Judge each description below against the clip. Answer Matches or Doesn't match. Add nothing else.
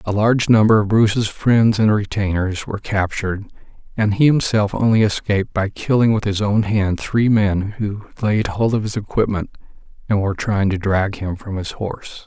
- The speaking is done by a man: Matches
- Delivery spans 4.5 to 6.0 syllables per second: Matches